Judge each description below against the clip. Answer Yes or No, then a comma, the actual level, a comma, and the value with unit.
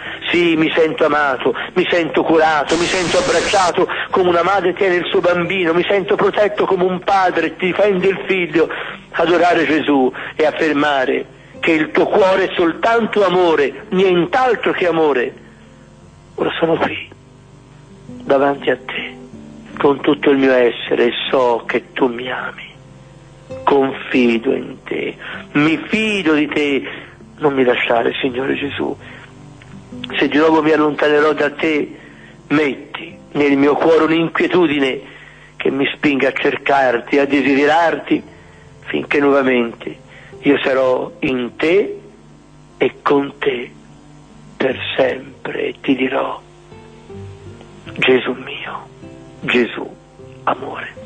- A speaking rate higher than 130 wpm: No, average, 125 wpm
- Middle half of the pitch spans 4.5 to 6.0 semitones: Yes, average, 5.2 semitones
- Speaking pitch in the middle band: Yes, medium, 155 Hz